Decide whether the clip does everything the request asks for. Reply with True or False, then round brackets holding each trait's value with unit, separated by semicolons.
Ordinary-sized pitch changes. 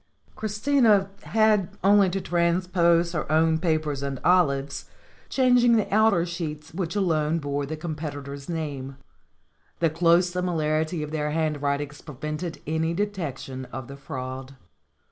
True (3.8 semitones)